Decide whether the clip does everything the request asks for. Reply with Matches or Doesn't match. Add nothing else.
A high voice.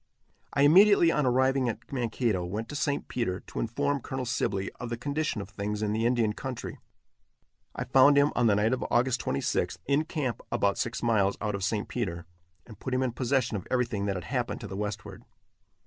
Doesn't match